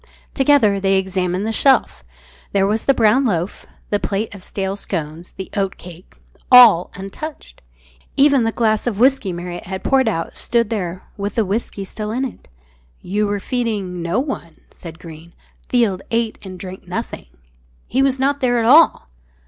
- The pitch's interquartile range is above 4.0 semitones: Yes, average, 4.7 semitones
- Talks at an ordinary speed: Yes, average, 165 wpm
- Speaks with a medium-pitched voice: No, high, 205 Hz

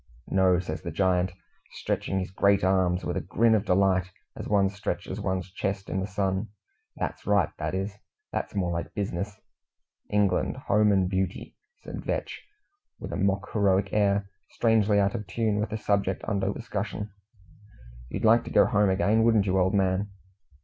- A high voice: No, low, 100 Hz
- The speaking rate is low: No, average, 170 wpm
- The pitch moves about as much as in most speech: No, narrow, 1.7 semitones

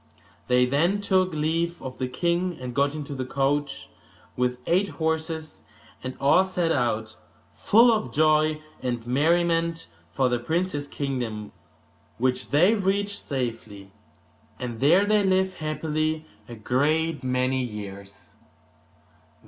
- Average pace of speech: No, slow, 125 wpm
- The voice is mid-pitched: Yes, medium, 145 Hz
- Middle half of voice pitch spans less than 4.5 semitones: No, average, 5.1 semitones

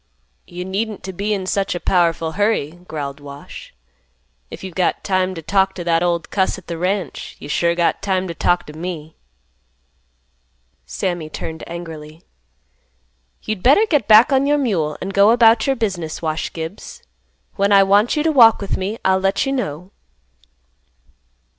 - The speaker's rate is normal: Yes, average, 170 wpm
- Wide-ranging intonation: No, average, 3.8 semitones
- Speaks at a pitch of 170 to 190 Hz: Yes, medium, 185 Hz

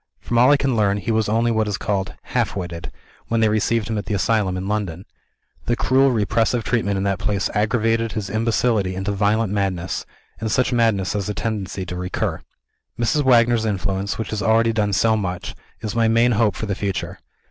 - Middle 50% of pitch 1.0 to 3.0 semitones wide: Yes, average, 2.7 semitones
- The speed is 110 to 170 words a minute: No, average, 200 wpm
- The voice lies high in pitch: No, low, 105 Hz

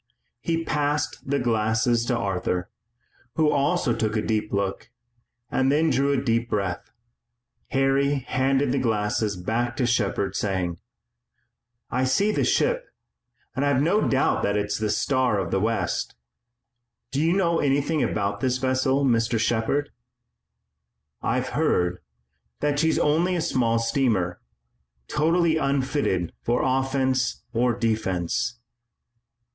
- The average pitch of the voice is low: Yes, low, 125 Hz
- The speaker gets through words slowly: Yes, slow, 130 wpm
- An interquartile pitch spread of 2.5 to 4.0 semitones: No, average, 4.5 semitones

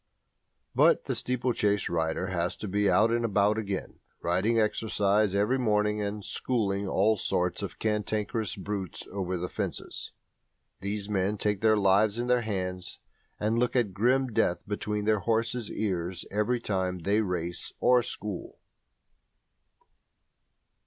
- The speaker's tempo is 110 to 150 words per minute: Yes, average, 140 wpm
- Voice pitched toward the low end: Yes, low, 105 Hz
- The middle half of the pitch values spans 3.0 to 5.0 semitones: No, narrow, 2.6 semitones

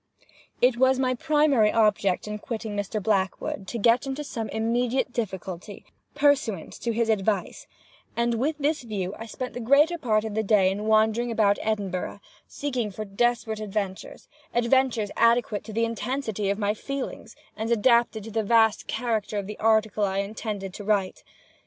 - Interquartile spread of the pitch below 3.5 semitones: Yes, average, 2.8 semitones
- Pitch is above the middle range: Yes, high, 220 Hz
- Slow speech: No, average, 165 wpm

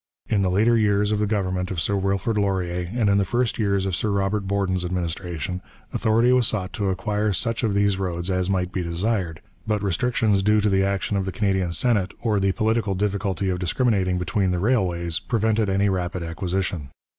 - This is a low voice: Yes, low, 100 Hz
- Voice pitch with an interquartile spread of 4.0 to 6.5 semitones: No, narrow, 2.5 semitones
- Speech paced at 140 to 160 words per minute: No, average, 200 wpm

